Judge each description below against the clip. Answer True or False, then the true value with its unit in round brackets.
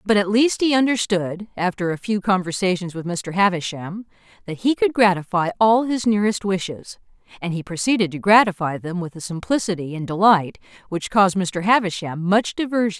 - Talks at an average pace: True (170 wpm)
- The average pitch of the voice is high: True (195 Hz)